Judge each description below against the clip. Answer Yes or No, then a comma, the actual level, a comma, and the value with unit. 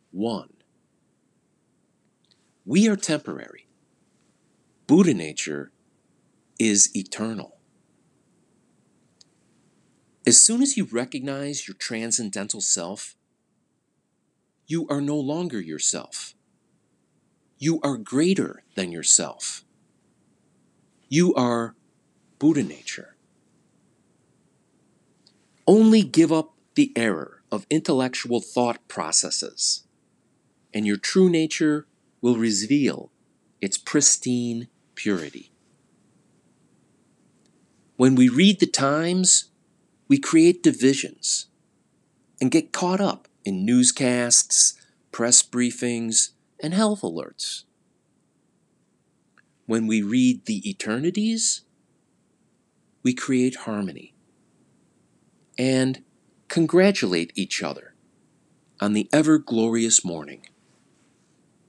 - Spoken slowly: Yes, slow, 80 wpm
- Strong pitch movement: Yes, wide, 7.8 semitones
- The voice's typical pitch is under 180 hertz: Yes, medium, 140 Hz